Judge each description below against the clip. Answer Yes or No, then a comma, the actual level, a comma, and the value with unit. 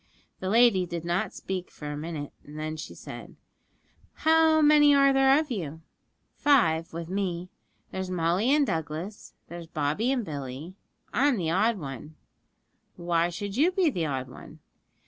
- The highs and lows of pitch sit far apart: Yes, wide, 7.7 semitones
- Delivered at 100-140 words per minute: No, average, 160 wpm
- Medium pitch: Yes, medium, 180 Hz